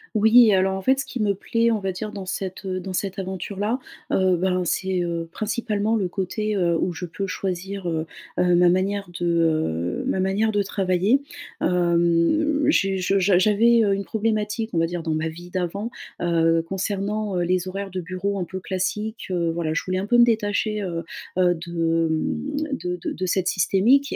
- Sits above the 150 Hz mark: Yes, high, 190 Hz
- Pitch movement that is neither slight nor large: Yes, average, 3.0 semitones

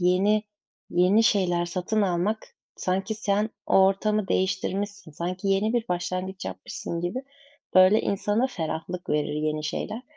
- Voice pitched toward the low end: No, high, 190 Hz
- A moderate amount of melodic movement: Yes, average, 3.0 semitones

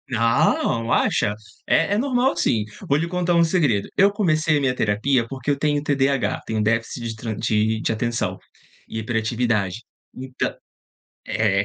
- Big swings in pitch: Yes, wide, 5.7 semitones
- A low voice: Yes, low, 125 Hz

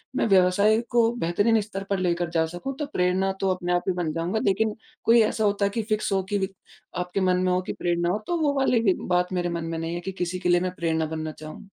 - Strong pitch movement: No, average, 2.9 semitones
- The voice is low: No, medium, 185 Hz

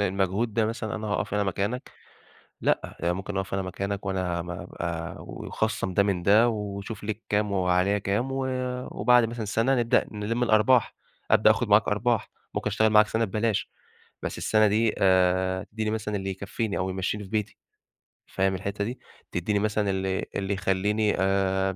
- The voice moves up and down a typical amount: No, narrow, 2.2 semitones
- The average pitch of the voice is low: Yes, low, 100 Hz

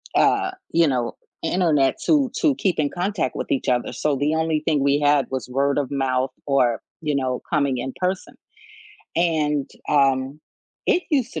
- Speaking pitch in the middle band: Yes, medium, 145 Hz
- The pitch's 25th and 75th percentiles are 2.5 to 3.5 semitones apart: No, average, 3.9 semitones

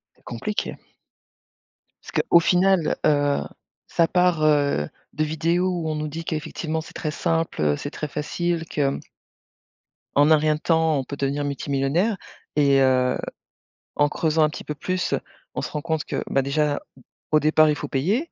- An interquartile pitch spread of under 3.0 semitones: Yes, narrow, 2.4 semitones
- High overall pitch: No, medium, 155 Hz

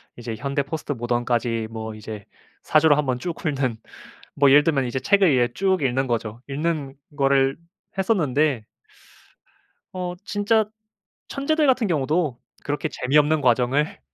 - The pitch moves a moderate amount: Yes, average, 4.7 semitones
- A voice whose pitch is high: No, medium, 140 Hz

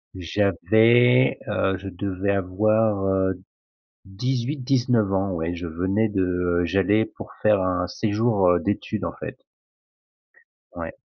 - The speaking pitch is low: Yes, low, 100 Hz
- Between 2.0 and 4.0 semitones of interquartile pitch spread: Yes, average, 3.1 semitones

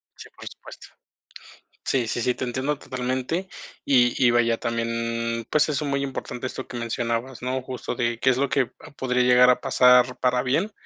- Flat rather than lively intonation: Yes, narrow, 1.8 semitones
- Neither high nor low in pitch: No, low, 125 Hz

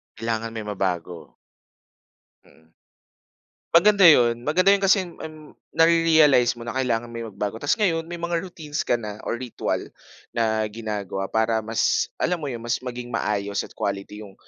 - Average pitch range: No, wide, 6.8 semitones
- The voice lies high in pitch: No, low, 120 Hz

